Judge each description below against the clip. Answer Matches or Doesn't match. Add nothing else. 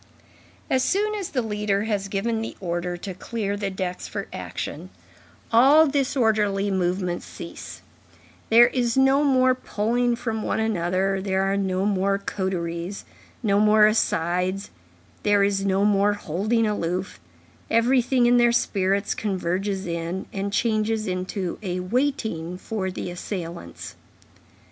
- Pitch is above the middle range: Matches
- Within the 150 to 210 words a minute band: Doesn't match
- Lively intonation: Doesn't match